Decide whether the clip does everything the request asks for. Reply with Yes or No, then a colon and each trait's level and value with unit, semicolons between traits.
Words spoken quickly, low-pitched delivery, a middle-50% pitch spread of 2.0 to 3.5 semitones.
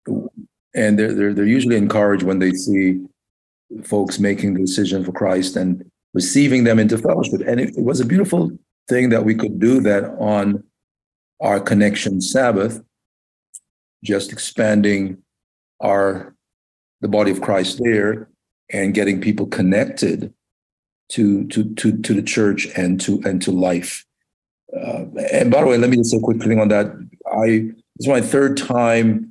No: average, 160 wpm; low, 105 Hz; average, 2.9 semitones